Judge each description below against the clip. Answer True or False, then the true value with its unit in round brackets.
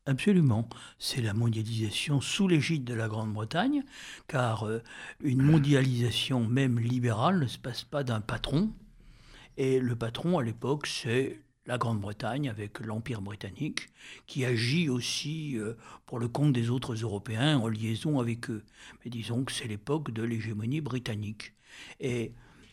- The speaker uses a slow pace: True (140 wpm)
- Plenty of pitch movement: False (3.9 semitones)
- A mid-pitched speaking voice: False (125 Hz)